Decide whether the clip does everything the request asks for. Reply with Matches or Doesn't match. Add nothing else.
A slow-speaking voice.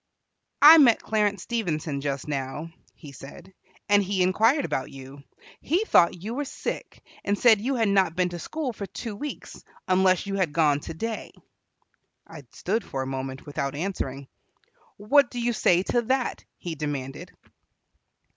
Doesn't match